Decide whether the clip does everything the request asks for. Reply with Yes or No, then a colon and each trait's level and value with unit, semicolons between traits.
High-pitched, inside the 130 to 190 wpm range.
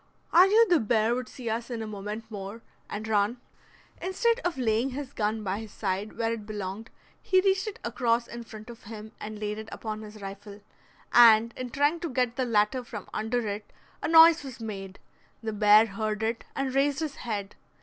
No: high, 225 Hz; average, 200 wpm